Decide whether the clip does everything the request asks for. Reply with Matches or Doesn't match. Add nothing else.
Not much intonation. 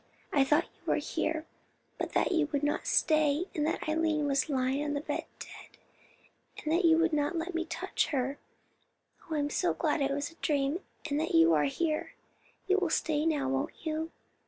Matches